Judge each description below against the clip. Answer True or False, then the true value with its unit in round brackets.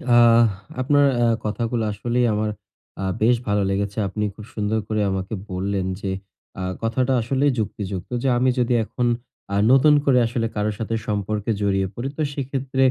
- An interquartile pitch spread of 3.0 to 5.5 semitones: True (3.5 semitones)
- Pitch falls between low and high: False (115 Hz)